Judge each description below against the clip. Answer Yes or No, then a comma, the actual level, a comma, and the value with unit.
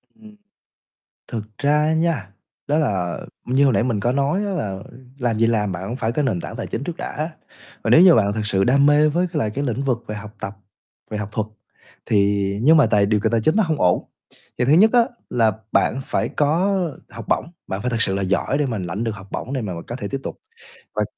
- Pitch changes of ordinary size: No, wide, 6.2 semitones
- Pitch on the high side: No, low, 120 Hz